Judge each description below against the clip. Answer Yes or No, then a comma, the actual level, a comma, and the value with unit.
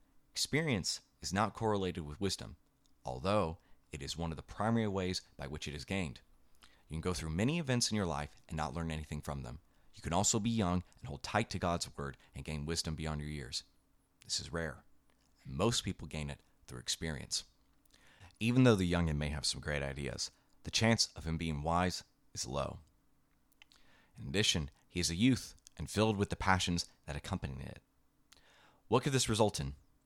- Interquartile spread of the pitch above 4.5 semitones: Yes, wide, 5.6 semitones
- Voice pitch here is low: Yes, very low, 85 Hz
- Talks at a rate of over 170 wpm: Yes, average, 195 wpm